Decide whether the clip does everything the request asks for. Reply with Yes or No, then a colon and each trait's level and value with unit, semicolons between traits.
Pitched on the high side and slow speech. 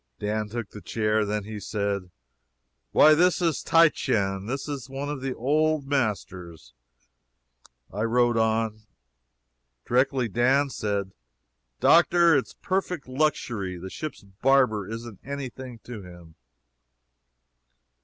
No: low, 115 Hz; slow, 125 wpm